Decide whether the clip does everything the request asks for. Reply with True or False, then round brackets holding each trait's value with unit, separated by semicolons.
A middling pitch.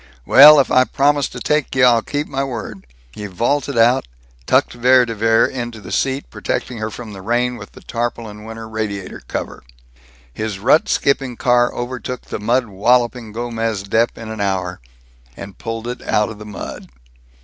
False (115 Hz)